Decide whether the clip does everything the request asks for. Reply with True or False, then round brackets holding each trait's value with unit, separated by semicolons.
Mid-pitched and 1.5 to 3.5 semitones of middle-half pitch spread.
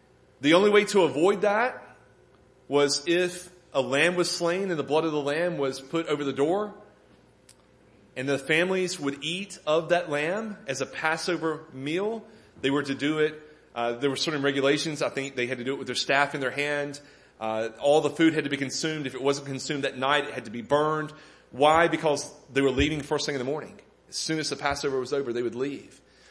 True (145 Hz; 2.9 semitones)